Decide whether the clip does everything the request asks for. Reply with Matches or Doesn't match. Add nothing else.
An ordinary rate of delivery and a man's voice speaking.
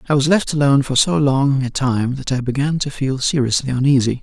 Doesn't match